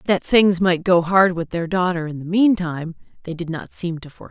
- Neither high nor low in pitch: Yes, medium, 175 Hz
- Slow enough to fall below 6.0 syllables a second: Yes, 5.6 syllables/s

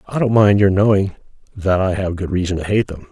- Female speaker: No, male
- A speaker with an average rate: No, fast, 250 wpm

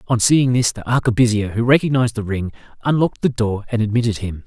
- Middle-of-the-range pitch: No, low, 115 Hz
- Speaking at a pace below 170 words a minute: No, average, 200 wpm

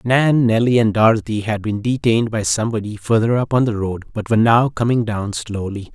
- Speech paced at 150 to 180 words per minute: No, average, 200 wpm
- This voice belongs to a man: Yes, male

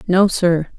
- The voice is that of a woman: Yes, female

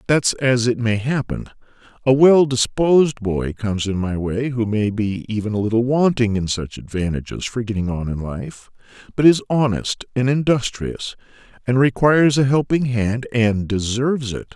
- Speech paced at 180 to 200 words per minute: No, average, 170 wpm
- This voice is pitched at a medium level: No, low, 120 Hz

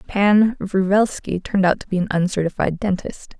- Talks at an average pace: Yes, average, 160 wpm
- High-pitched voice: Yes, high, 195 Hz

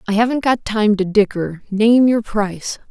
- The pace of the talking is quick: No, average, 165 wpm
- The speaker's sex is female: Yes, female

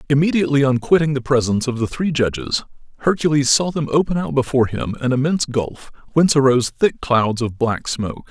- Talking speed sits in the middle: Yes, average, 190 wpm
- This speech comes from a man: Yes, male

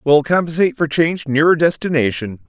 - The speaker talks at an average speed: Yes, average, 145 wpm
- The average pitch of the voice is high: No, medium, 155 Hz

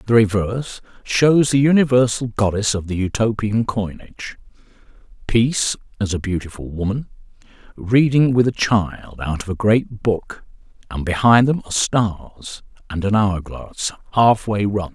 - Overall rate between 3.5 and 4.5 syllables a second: Yes, 4.4 syllables/s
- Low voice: Yes, low, 110 Hz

